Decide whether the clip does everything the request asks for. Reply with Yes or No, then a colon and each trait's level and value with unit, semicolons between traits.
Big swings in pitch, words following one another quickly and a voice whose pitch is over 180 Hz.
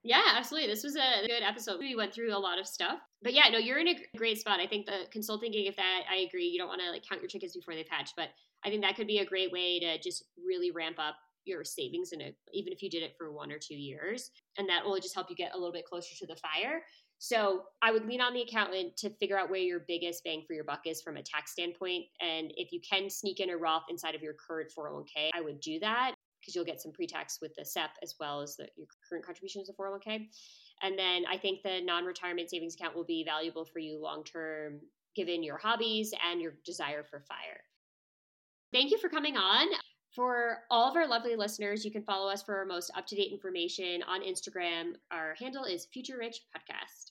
No: average, 5.0 semitones; fast, 250 wpm; high, 190 Hz